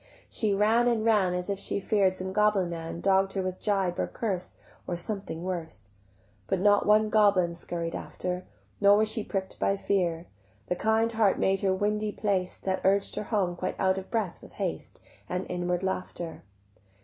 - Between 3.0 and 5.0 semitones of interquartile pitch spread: No, narrow, 2.6 semitones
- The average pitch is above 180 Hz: Yes, high, 190 Hz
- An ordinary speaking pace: Yes, average, 185 wpm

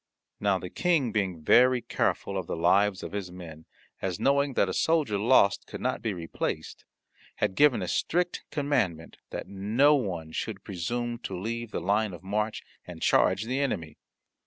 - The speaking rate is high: No, average, 175 wpm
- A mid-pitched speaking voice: No, low, 100 Hz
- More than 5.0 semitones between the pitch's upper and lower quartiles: Yes, wide, 5.5 semitones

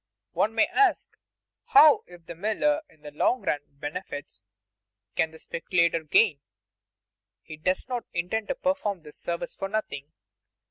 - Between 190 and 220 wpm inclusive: No, average, 145 wpm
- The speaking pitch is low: No, medium, 175 Hz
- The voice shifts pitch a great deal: Yes, wide, 6.0 semitones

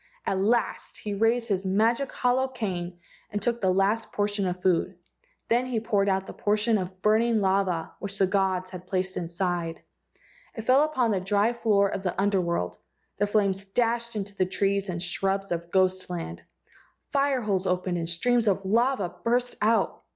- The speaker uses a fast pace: No, average, 180 wpm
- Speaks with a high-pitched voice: Yes, high, 200 Hz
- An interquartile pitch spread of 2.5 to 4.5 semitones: Yes, average, 3.5 semitones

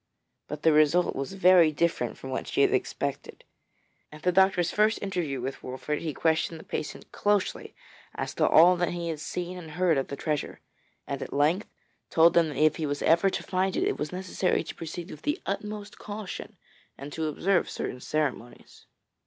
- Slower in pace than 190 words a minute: No, average, 195 wpm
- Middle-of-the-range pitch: Yes, medium, 165 Hz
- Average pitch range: Yes, average, 3.5 semitones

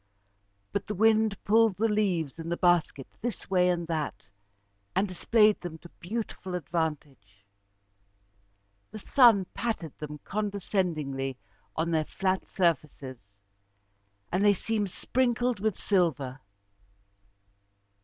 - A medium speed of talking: No, slow, 115 wpm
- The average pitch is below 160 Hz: No, medium, 180 Hz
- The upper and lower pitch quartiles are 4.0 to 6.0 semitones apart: Yes, average, 5.1 semitones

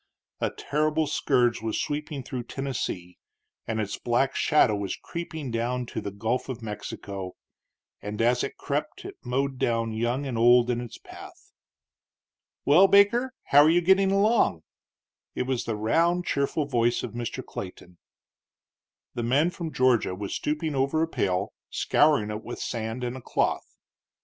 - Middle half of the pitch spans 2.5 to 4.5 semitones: No, average, 5.0 semitones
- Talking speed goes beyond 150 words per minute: Yes, average, 160 wpm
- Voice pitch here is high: No, low, 125 Hz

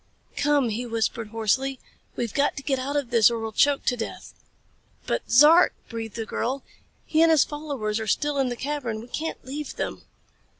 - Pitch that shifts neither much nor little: Yes, average, 4.2 semitones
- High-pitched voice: Yes, very high, 255 Hz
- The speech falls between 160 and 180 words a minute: No, average, 195 wpm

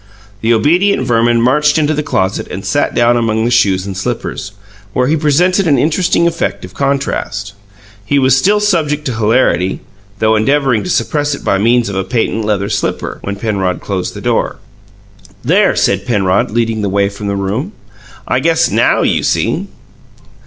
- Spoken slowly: No, average, 175 wpm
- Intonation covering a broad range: Yes, wide, 6.4 semitones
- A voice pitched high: No, low, 115 Hz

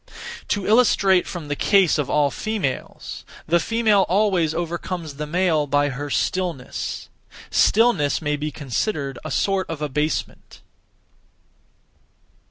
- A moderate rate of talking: No, slow, 120 wpm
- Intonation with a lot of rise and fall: No, average, 4.9 semitones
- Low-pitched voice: No, medium, 165 Hz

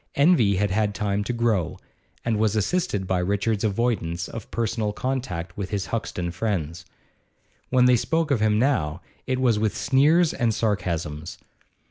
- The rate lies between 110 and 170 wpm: Yes, average, 155 wpm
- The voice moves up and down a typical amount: Yes, average, 4.5 semitones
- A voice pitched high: No, low, 105 Hz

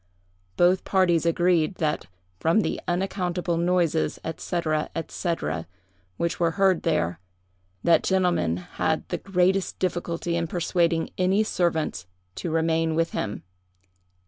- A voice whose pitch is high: No, medium, 170 Hz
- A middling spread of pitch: No, narrow, 1.9 semitones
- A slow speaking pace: Yes, slow, 120 wpm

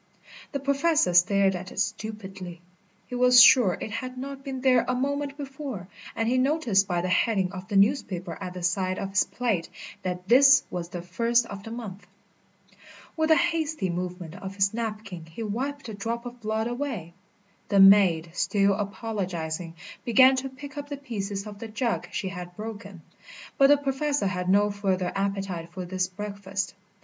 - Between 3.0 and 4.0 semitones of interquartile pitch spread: No, average, 5.3 semitones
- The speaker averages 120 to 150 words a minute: No, average, 180 wpm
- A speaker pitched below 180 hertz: No, high, 205 Hz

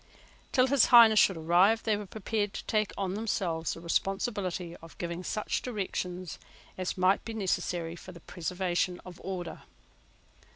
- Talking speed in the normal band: Yes, average, 155 wpm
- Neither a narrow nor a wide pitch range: Yes, average, 3.4 semitones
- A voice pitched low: No, medium, 185 Hz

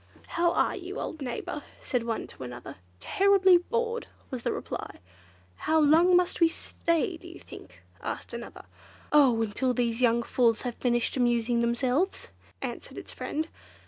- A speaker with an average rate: Yes, average, 155 wpm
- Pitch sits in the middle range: No, very high, 270 Hz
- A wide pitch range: Yes, wide, 6.6 semitones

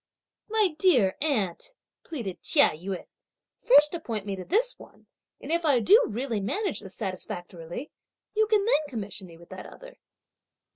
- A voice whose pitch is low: No, very high, 260 Hz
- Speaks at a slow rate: No, average, 155 wpm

